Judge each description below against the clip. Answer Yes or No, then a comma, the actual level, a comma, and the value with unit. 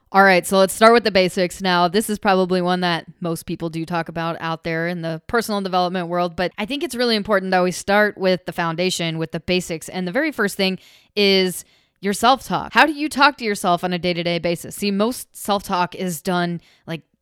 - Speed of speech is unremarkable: No, fast, 240 wpm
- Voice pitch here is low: No, medium, 185 Hz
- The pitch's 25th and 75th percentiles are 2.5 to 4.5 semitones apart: Yes, average, 2.9 semitones